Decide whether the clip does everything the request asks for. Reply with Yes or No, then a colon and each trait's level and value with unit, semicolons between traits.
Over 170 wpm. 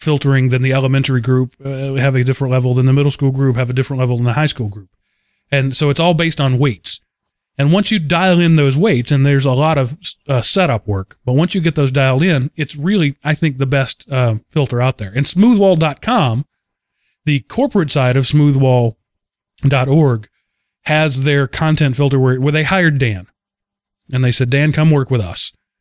Yes: average, 200 wpm